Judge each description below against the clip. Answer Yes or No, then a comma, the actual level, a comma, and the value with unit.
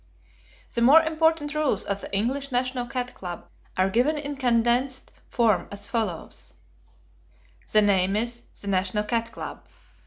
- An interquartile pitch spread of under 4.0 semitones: No, average, 4.8 semitones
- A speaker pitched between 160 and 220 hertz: No, high, 240 Hz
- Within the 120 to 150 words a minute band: Yes, average, 145 wpm